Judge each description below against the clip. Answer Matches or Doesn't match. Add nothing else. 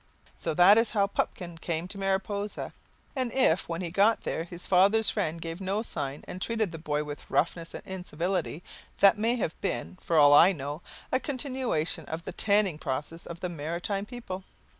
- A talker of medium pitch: Matches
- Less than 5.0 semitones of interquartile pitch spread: Matches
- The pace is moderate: Matches